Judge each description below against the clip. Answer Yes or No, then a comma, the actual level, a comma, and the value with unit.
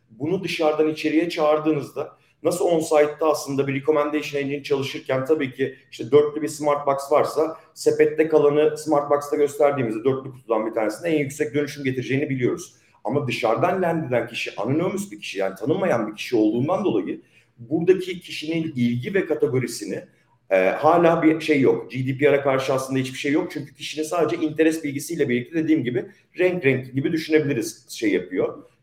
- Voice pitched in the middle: Yes, medium, 150 Hz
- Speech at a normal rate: No, fast, 160 wpm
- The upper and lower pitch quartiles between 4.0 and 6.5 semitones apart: No, average, 2.7 semitones